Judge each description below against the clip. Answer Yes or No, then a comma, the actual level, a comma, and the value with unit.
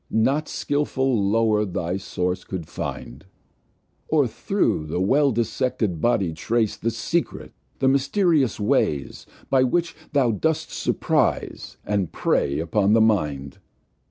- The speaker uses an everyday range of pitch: No, wide, 6.5 semitones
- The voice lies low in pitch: Yes, low, 110 Hz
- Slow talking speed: Yes, slow, 125 wpm